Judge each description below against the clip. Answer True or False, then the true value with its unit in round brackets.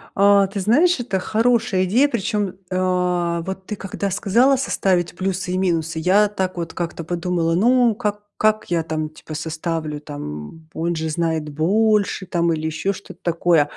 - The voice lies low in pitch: False (180 Hz)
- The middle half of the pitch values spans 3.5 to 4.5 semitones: True (4.0 semitones)